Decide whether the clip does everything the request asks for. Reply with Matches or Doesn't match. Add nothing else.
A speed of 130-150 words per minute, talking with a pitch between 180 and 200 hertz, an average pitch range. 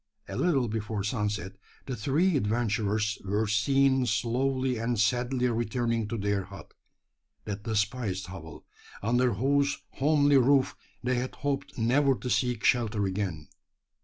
Doesn't match